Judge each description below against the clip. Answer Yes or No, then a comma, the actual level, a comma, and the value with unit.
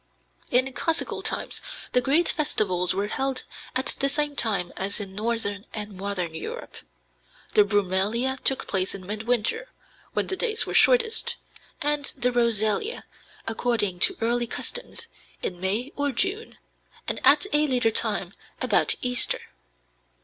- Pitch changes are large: Yes, wide, 5.7 semitones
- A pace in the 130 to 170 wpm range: Yes, average, 140 wpm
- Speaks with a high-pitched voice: Yes, high, 235 Hz